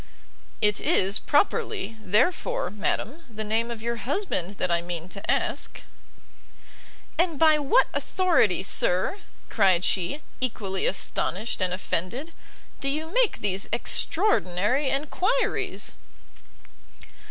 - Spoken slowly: Yes, slow, 110 wpm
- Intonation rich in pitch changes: Yes, wide, 8.6 semitones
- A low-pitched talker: No, high, 230 Hz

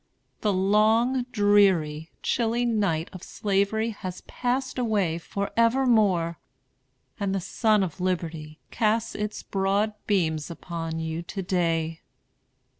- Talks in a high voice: Yes, high, 195 Hz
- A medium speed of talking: No, slow, 115 wpm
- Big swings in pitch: No, average, 4.6 semitones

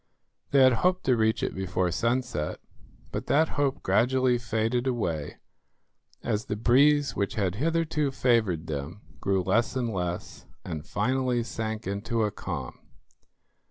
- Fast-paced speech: No, average, 140 wpm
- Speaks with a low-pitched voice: Yes, low, 115 Hz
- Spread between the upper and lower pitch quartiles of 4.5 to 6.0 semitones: Yes, average, 4.9 semitones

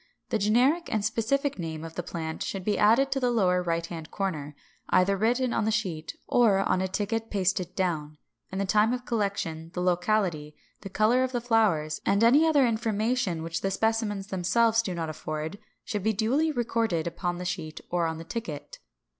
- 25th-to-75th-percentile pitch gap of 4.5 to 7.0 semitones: Yes, average, 4.9 semitones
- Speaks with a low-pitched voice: No, high, 200 Hz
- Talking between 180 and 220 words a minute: Yes, average, 190 wpm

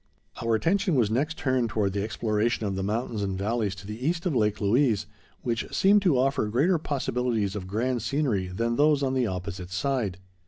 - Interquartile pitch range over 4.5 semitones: Yes, average, 4.9 semitones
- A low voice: Yes, low, 115 Hz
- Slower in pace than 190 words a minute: No, average, 195 wpm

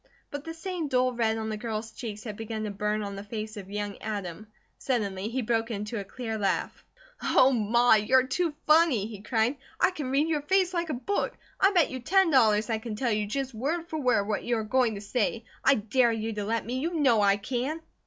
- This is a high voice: Yes, high, 230 Hz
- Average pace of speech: No, fast, 230 wpm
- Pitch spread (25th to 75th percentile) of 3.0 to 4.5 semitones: Yes, average, 4.2 semitones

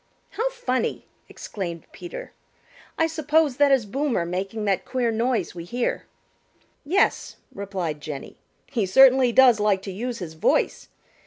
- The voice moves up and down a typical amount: No, wide, 6.1 semitones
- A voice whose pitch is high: Yes, high, 235 Hz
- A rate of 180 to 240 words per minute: No, average, 140 wpm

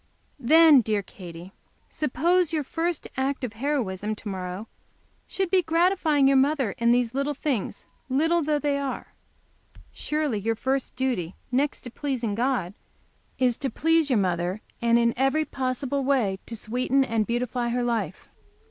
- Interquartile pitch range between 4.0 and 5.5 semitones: Yes, average, 4.4 semitones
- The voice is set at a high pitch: Yes, very high, 255 Hz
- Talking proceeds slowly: No, average, 155 wpm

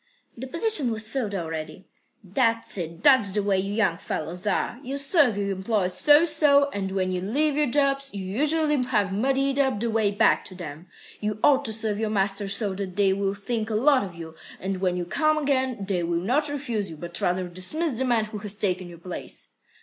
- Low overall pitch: No, high, 210 Hz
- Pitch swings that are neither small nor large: No, wide, 6.1 semitones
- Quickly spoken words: Yes, fast, 215 wpm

